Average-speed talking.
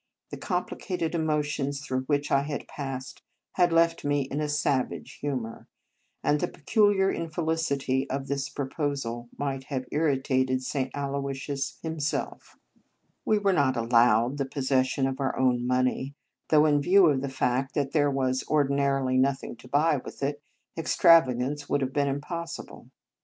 Yes: average, 155 wpm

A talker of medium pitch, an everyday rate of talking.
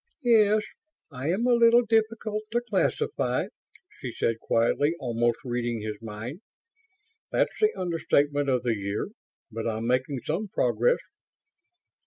No: medium, 145 Hz; slow, 130 wpm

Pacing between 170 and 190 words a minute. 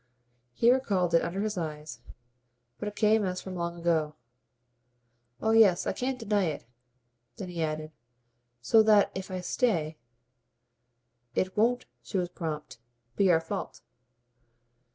No: average, 145 wpm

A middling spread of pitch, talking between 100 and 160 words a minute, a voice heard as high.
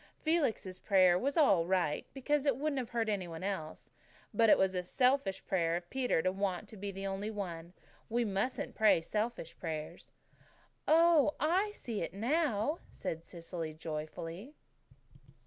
No: wide, 6.9 semitones; average, 155 wpm; high, 200 Hz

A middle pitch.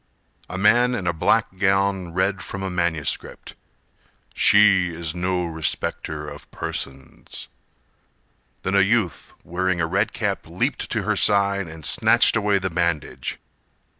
No: very low, 95 Hz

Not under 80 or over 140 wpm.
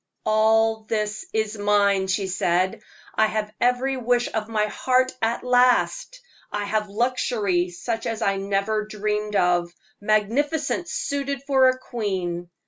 Yes: slow, 135 wpm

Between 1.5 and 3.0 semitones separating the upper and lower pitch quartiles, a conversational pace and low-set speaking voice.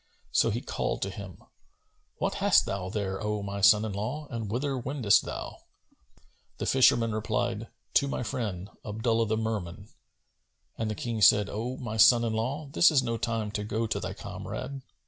Yes: narrow, 2.4 semitones; average, 180 wpm; low, 110 Hz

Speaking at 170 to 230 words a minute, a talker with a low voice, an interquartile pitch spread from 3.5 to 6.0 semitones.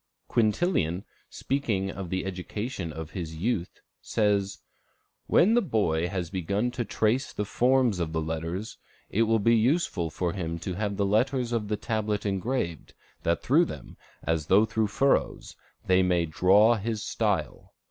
No: average, 150 wpm; low, 100 Hz; average, 4.7 semitones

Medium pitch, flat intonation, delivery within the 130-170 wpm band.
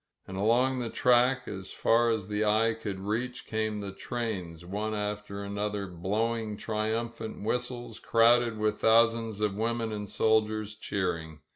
No: low, 110 Hz; narrow, 2.1 semitones; average, 145 wpm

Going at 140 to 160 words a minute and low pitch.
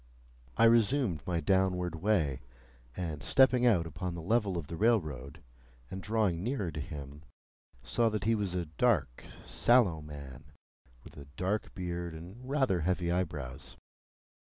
Yes: average, 145 wpm; very low, 90 Hz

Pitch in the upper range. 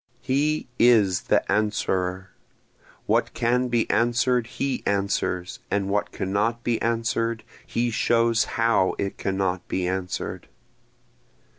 No: low, 115 Hz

